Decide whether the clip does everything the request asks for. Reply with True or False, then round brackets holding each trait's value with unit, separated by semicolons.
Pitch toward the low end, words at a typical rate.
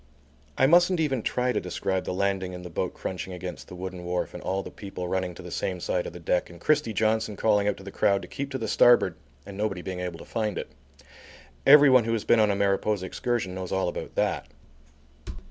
False (100 Hz; 230 wpm)